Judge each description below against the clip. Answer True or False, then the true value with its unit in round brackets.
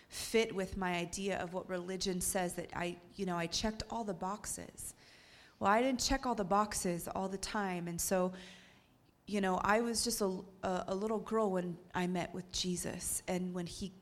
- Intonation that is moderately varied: False (2.3 semitones)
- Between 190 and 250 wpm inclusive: True (200 wpm)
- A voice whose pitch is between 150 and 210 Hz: True (190 Hz)